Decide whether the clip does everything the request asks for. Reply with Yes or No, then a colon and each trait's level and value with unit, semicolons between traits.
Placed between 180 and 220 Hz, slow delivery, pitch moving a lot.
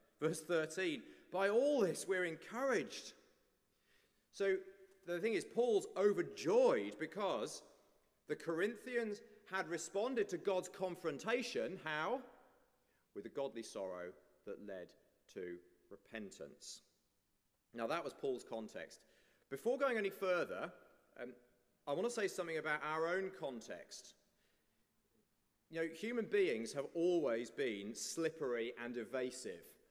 Yes: high, 190 Hz; slow, 120 wpm; wide, 7.9 semitones